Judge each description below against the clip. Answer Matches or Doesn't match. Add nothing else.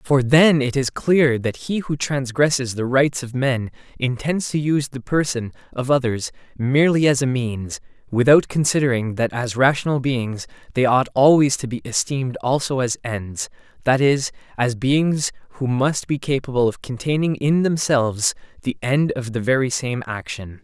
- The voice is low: Matches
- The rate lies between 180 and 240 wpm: Doesn't match